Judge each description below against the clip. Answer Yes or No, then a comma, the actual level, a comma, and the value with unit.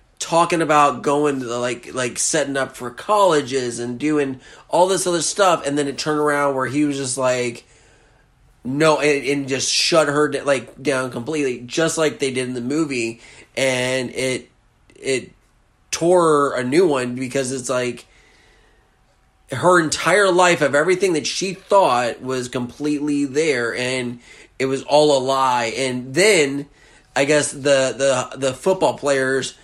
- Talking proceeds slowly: No, average, 160 wpm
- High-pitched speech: No, medium, 140 Hz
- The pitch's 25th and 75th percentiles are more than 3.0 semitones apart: No, average, 2.7 semitones